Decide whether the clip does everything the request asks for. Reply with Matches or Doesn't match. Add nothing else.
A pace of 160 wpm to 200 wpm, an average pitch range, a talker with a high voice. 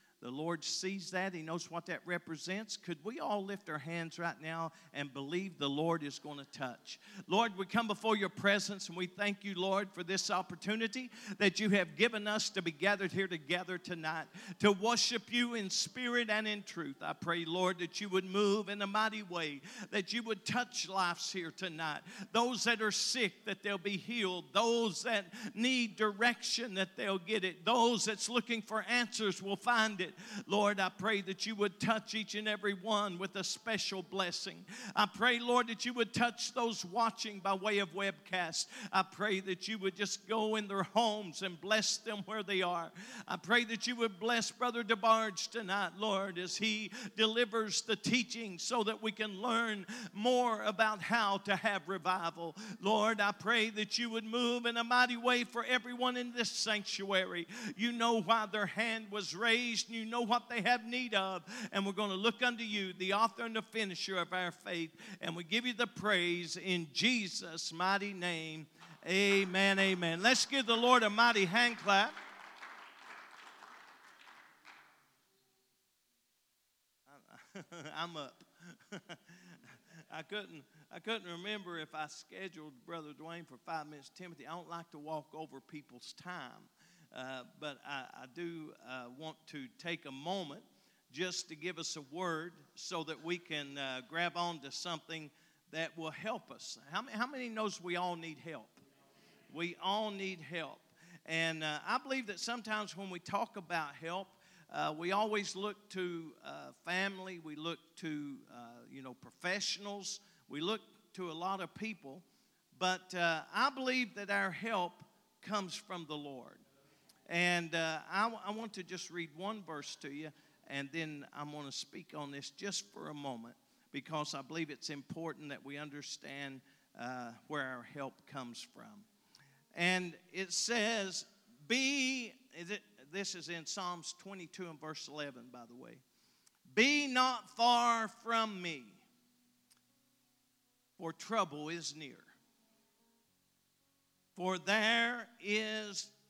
Matches